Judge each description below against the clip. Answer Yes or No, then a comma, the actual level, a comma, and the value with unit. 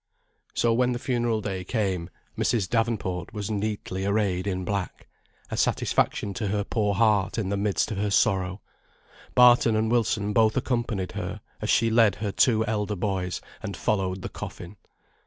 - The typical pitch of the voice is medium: No, low, 105 Hz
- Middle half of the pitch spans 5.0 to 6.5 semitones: No, average, 2.8 semitones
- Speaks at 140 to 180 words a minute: Yes, average, 165 wpm